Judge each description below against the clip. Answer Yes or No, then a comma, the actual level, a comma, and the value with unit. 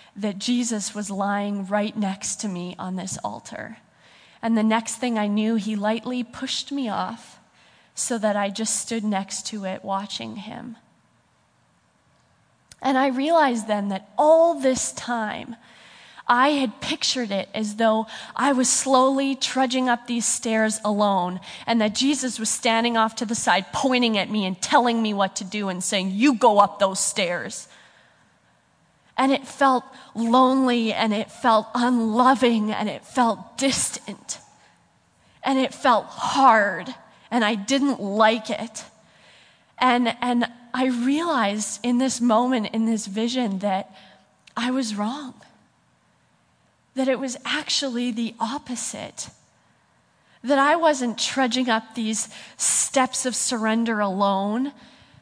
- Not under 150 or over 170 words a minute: No, average, 140 wpm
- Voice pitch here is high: Yes, high, 230 Hz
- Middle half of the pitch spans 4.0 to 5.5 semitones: No, average, 3.5 semitones